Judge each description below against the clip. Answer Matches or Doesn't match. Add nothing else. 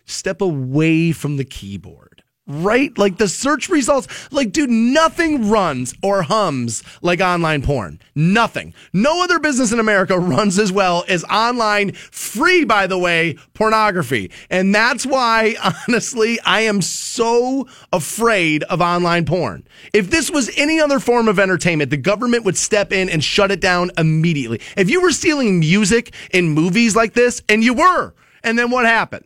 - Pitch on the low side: Doesn't match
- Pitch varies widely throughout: Matches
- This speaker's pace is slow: Doesn't match